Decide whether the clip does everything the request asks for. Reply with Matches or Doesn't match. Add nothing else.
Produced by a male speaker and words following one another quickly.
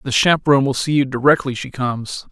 Matches